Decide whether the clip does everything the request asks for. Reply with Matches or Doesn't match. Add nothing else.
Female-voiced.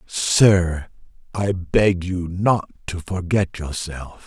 Doesn't match